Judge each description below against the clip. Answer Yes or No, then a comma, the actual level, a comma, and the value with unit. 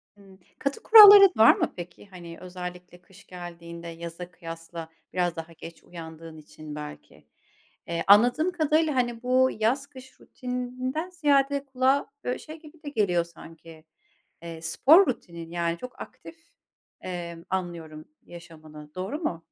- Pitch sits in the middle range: Yes, medium, 180 Hz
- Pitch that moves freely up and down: Yes, wide, 7.7 semitones